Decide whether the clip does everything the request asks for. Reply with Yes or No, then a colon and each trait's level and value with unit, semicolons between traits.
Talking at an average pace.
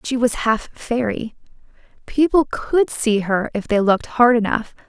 Yes: average, 160 wpm